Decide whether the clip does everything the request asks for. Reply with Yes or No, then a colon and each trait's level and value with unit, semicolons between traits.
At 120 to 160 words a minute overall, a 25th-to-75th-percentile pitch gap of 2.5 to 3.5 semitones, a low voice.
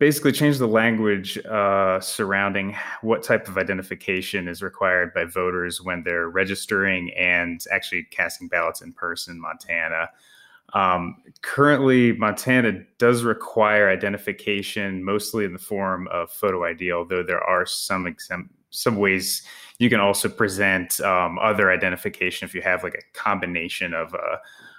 Yes: average, 145 wpm; average, 2.8 semitones; low, 100 Hz